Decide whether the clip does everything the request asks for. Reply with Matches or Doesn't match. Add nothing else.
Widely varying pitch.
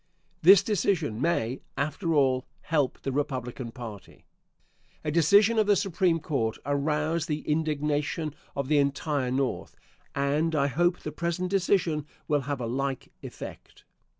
Doesn't match